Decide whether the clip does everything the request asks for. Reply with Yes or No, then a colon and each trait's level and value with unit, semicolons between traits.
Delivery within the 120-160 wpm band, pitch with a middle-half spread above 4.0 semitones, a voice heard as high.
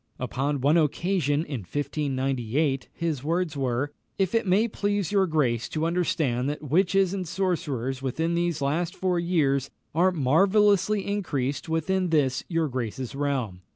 No: average, 140 wpm; average, 5.0 semitones; medium, 155 Hz